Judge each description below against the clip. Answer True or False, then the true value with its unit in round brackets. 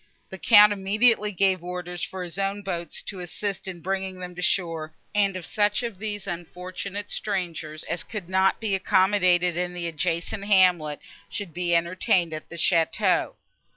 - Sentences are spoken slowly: False (165 wpm)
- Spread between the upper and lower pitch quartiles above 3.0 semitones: False (2.4 semitones)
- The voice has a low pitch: False (185 Hz)